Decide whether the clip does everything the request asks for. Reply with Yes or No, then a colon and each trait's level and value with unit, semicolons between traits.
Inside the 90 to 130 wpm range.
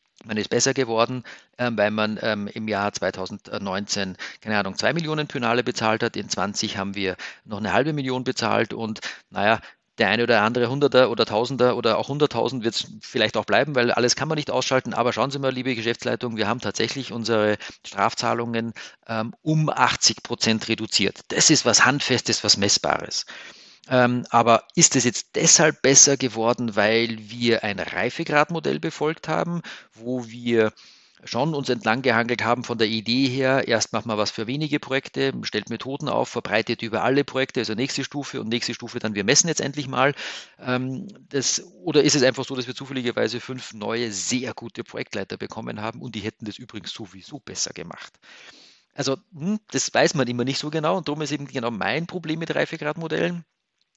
No: average, 180 wpm